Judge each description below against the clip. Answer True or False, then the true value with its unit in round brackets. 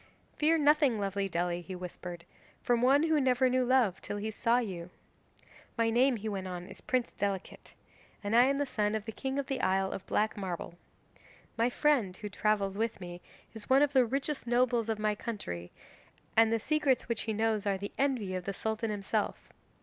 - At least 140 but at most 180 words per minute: False (200 wpm)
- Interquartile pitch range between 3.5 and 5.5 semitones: True (4.5 semitones)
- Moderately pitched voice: False (220 Hz)